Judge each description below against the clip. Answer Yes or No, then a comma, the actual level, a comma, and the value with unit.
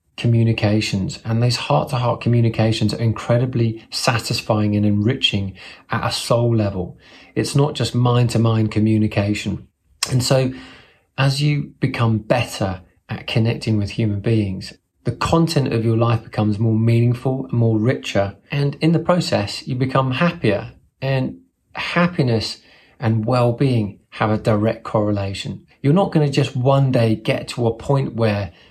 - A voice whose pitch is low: Yes, low, 115 Hz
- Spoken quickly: No, average, 140 wpm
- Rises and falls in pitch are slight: No, average, 3.6 semitones